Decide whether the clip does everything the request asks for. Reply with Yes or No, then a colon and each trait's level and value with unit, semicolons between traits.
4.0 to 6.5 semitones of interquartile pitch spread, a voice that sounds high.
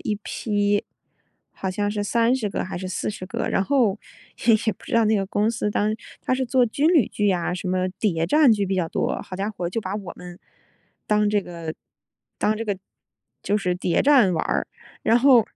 No: average, 3.4 semitones; high, 205 Hz